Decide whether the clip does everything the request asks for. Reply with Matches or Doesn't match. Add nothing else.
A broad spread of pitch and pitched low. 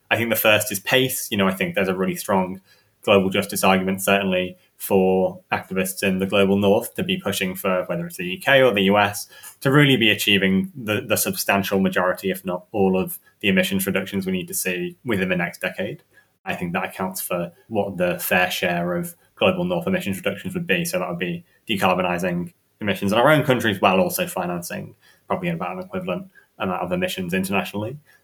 Matches